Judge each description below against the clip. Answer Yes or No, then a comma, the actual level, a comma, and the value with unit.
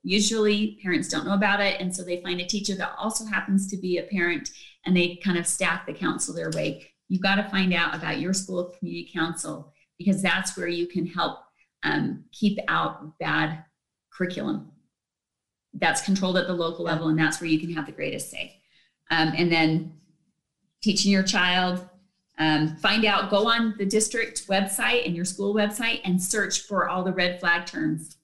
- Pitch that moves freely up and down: No, average, 3.0 semitones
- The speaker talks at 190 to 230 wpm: Yes, average, 195 wpm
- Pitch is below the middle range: No, medium, 185 Hz